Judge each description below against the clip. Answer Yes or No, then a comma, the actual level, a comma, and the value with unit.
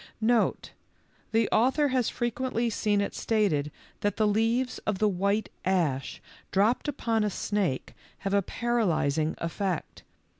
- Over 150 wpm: No, slow, 135 wpm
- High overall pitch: Yes, high, 210 Hz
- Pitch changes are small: No, average, 3.5 semitones